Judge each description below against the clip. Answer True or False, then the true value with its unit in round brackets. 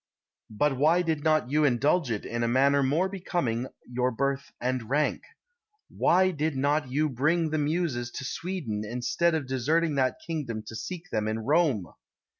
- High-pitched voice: False (140 Hz)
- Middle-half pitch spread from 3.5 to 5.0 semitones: True (4.5 semitones)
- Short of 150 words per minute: False (170 wpm)